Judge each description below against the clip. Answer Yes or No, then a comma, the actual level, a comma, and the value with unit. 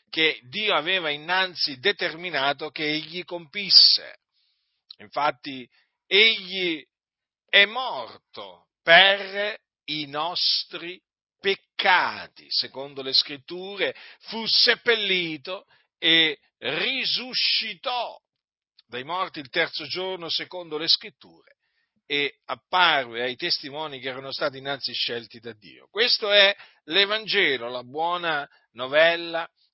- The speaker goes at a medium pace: No, slow, 95 wpm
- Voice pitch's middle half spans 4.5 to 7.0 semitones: Yes, average, 5.2 semitones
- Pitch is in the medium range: Yes, medium, 165 Hz